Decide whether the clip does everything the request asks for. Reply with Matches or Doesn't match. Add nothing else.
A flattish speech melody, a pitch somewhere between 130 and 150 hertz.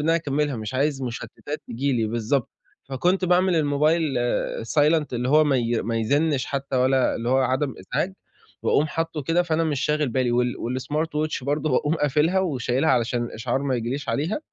Doesn't match